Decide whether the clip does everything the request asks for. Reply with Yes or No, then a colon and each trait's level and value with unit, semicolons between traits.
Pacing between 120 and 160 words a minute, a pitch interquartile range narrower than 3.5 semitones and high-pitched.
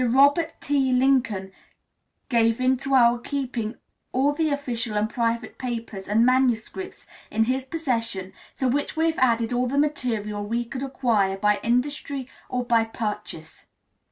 Yes: average, 145 wpm; average, 3.1 semitones; high, 245 Hz